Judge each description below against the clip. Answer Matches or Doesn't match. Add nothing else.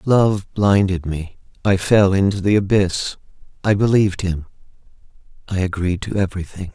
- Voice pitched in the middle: Doesn't match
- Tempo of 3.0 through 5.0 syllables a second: Matches